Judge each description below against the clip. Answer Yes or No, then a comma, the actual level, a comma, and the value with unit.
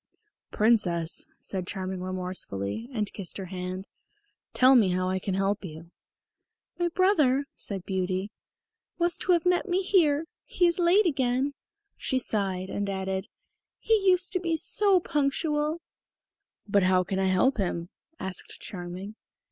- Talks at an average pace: Yes, average, 145 wpm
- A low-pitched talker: No, high, 205 Hz